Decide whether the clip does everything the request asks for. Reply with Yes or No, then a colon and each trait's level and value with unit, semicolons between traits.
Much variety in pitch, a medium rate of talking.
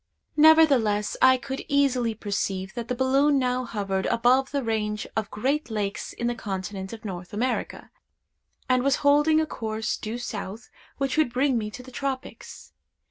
No: average, 4.2 semitones; average, 165 wpm